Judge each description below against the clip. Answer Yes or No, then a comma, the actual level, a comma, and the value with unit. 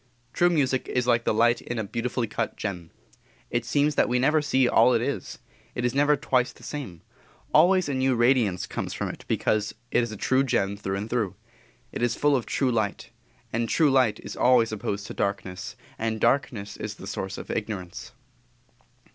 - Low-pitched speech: Yes, low, 120 Hz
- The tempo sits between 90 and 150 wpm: No, average, 195 wpm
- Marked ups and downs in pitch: No, average, 3.9 semitones